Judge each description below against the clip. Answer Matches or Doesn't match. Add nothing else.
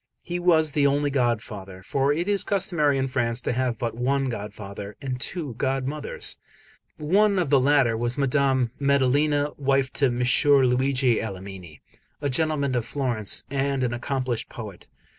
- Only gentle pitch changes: Doesn't match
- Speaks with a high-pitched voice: Doesn't match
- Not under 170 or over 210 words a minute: Doesn't match